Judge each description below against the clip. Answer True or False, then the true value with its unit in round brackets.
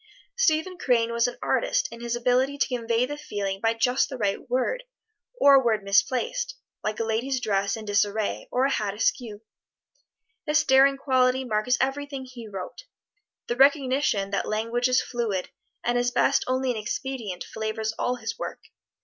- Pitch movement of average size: True (3.4 semitones)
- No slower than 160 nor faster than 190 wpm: True (170 wpm)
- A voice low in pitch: False (245 Hz)